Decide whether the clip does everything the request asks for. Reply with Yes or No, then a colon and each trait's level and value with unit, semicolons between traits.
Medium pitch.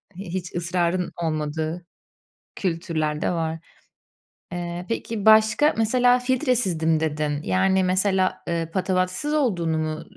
Yes: medium, 180 Hz